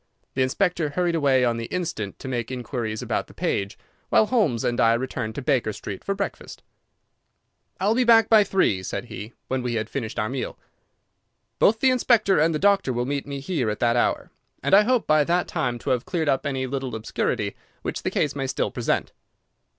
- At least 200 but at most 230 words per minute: Yes, fast, 205 wpm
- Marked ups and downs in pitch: Yes, wide, 7.3 semitones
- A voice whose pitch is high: No, low, 135 Hz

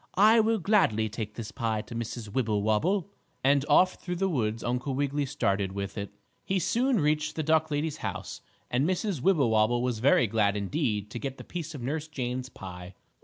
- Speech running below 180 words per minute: No, average, 185 wpm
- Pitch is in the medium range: No, low, 130 Hz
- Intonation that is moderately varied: No, wide, 6.6 semitones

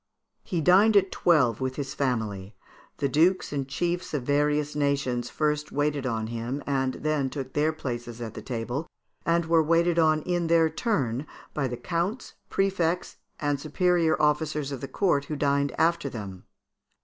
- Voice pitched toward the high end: No, medium, 145 Hz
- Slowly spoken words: No, average, 165 wpm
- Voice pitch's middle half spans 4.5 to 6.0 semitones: No, average, 4.1 semitones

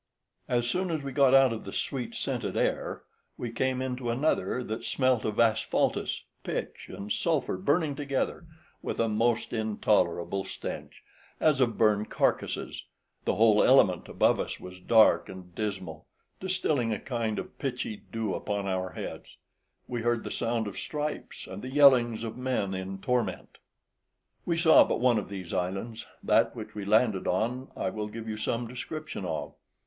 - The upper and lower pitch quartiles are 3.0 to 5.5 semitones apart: Yes, average, 4.0 semitones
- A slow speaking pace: No, average, 165 wpm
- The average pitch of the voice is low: Yes, low, 115 Hz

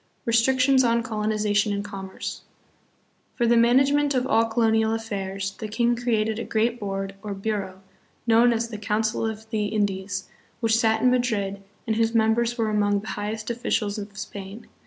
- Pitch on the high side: Yes, high, 220 Hz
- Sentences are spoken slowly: No, average, 170 wpm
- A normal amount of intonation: No, narrow, 2.2 semitones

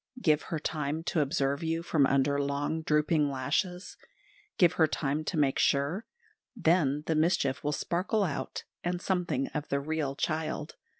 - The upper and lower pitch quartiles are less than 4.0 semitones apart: Yes, average, 3.3 semitones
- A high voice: No, medium, 155 Hz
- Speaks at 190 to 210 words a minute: No, average, 160 wpm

